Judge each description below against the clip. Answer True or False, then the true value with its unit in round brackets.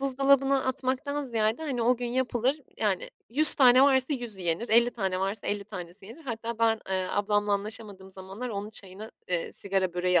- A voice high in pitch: True (225 Hz)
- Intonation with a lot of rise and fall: False (4.9 semitones)